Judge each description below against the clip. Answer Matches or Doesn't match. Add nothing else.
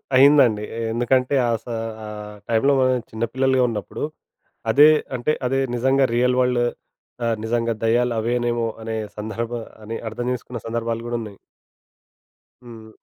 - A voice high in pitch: Doesn't match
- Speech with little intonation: Matches